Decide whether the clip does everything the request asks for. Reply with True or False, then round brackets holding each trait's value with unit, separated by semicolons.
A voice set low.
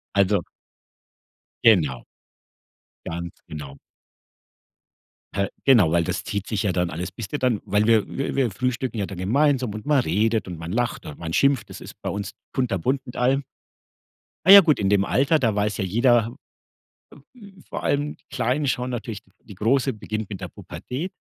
True (110 Hz)